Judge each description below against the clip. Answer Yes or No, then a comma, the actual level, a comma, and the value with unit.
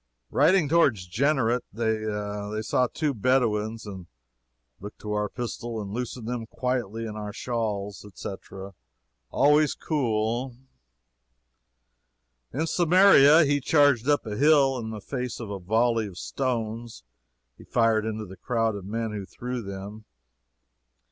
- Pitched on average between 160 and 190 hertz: No, low, 115 Hz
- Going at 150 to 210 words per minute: No, slow, 135 wpm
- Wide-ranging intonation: No, average, 3.6 semitones